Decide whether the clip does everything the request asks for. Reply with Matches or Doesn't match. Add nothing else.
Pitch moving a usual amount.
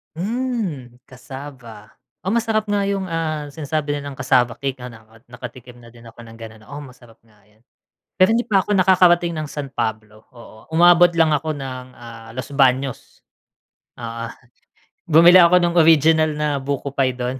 Doesn't match